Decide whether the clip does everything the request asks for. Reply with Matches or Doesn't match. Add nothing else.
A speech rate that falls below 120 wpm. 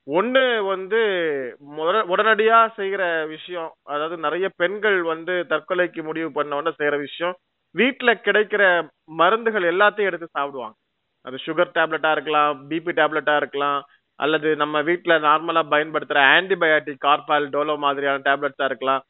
Doesn't match